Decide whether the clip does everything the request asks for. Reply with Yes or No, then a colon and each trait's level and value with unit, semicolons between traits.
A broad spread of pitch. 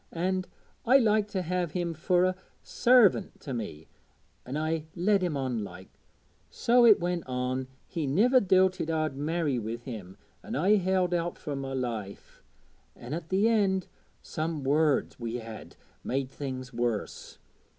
Yes: wide, 6.3 semitones